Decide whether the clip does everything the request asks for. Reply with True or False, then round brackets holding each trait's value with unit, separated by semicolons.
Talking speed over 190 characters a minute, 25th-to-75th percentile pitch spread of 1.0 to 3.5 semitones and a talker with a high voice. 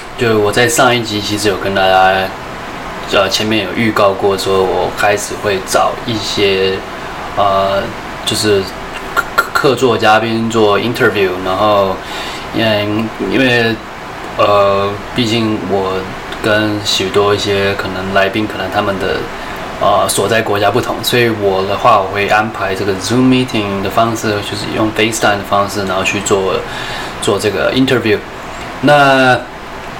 False (265 characters per minute; 2.4 semitones; 105 Hz)